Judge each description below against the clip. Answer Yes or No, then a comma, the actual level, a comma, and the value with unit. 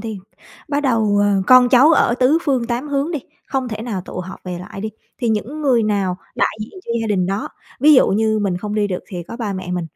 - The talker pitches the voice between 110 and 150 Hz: No, high, 220 Hz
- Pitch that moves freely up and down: No, average, 4.4 semitones